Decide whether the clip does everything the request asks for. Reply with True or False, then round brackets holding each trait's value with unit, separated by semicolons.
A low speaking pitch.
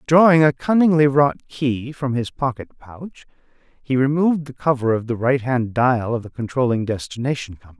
True (130 Hz)